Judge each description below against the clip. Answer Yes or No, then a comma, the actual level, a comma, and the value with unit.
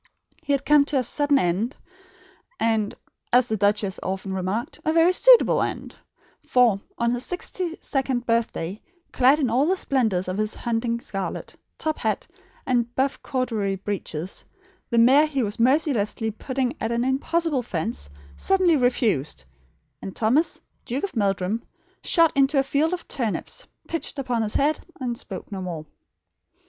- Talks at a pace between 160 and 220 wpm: No, average, 150 wpm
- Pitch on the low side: No, high, 240 Hz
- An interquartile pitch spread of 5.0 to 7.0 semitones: Yes, average, 5.3 semitones